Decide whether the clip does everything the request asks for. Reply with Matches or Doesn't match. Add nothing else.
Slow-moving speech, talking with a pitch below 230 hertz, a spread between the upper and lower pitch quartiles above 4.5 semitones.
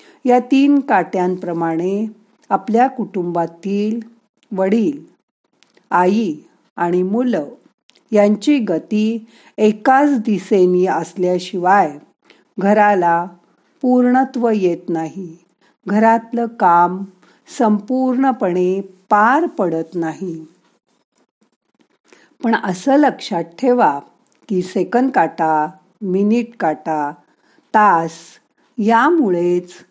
Matches